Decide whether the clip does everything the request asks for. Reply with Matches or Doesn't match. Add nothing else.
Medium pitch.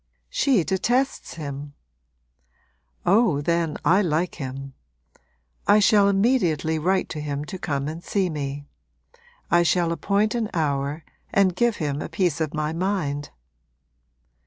Matches